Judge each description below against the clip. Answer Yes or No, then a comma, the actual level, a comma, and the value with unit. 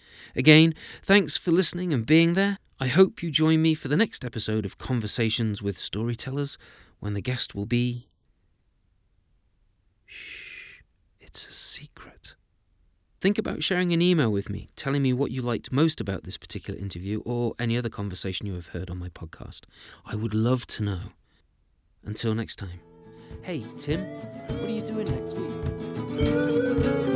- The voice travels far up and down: Yes, wide, 7.7 semitones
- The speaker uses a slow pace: No, average, 160 wpm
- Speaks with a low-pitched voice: Yes, low, 115 Hz